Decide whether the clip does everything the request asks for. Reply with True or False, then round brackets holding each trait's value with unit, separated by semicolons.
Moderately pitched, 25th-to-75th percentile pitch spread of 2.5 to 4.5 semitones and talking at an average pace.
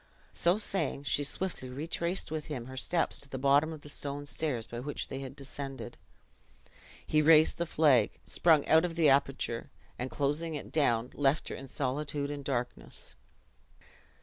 True (145 Hz; 2.8 semitones; 170 wpm)